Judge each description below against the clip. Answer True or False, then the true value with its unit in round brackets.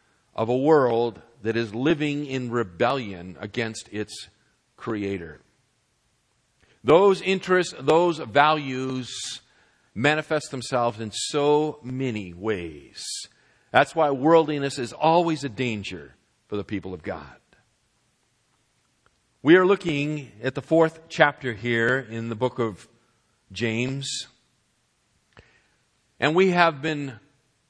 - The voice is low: True (130 Hz)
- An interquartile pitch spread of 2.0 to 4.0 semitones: False (5.1 semitones)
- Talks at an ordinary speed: False (110 wpm)